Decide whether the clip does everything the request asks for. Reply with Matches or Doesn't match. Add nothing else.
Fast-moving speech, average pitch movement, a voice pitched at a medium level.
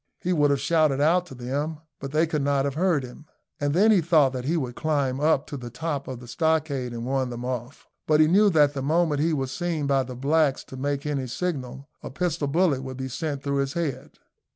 Matches